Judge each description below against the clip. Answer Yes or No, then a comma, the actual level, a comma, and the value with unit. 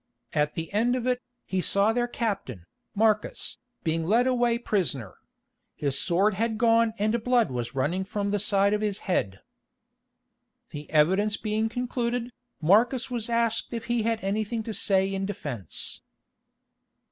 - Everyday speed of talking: Yes, average, 150 wpm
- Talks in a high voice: Yes, high, 210 Hz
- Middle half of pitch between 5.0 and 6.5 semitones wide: No, average, 3.8 semitones